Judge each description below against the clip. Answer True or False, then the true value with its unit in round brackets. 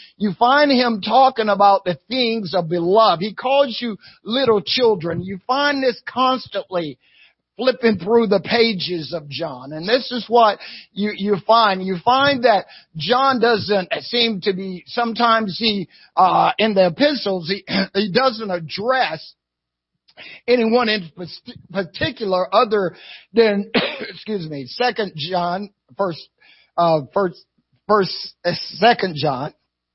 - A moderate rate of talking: False (130 wpm)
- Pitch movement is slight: False (4.9 semitones)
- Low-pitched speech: False (205 Hz)